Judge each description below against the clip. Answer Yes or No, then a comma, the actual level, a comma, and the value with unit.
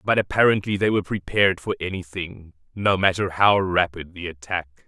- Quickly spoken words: No, average, 160 wpm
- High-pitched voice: No, very low, 95 Hz